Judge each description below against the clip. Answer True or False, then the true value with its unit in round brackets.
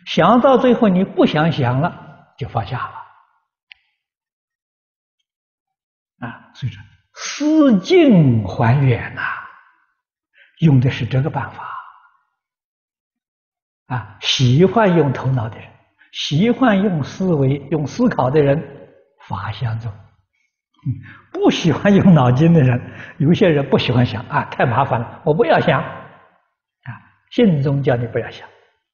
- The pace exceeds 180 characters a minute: False (170 characters per minute)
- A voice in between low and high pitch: True (150 Hz)